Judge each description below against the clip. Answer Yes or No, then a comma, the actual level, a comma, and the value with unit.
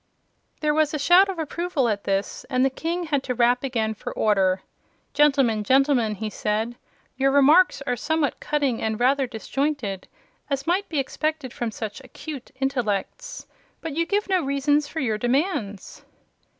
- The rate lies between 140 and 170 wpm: Yes, average, 165 wpm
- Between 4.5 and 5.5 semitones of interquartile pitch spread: Yes, average, 5.2 semitones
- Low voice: No, very high, 270 Hz